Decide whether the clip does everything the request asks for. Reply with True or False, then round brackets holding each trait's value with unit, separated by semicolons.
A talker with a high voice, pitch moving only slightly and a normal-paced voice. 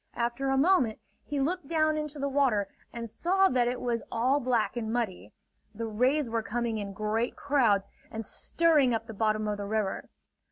False (240 Hz; 4.3 semitones; 190 wpm)